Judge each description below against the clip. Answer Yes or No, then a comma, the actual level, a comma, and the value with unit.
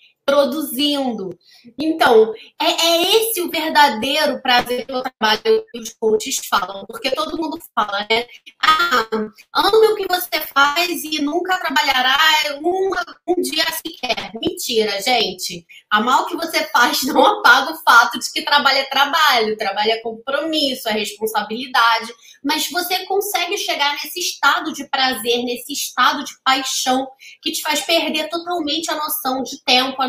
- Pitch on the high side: Yes, very high, 285 Hz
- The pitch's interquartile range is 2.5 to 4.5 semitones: No, average, 5.3 semitones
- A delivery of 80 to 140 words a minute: No, average, 150 wpm